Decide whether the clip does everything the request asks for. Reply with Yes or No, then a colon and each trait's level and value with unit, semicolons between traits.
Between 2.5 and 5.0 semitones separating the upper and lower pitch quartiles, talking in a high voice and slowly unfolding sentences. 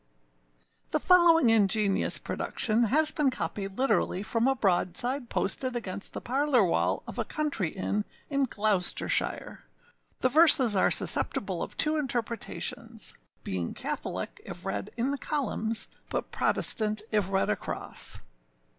No: wide, 5.5 semitones; high, 230 Hz; slow, 130 wpm